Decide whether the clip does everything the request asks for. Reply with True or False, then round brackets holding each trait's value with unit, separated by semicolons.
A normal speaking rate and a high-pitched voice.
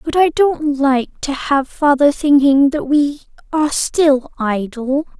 True (150 wpm; 285 Hz)